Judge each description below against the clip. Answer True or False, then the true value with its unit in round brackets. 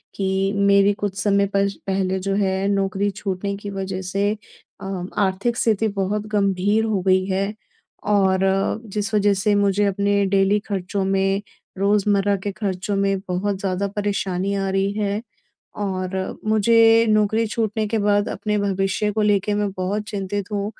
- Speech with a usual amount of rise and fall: False (1.2 semitones)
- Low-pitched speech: False (200 Hz)